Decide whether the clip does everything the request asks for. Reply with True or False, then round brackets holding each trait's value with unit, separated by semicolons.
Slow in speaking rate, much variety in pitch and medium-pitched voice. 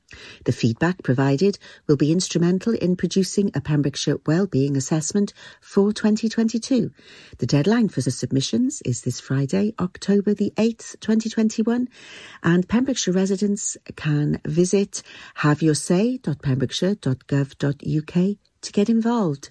True (110 wpm; 6.4 semitones; 180 Hz)